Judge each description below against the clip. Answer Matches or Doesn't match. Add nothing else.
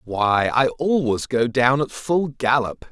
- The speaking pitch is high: Doesn't match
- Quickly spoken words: Doesn't match